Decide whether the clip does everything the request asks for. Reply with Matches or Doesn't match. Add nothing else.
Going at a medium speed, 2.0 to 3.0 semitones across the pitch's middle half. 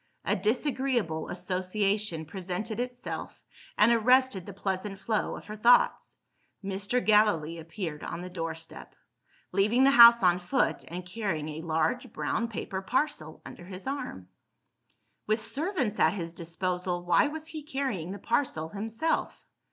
Doesn't match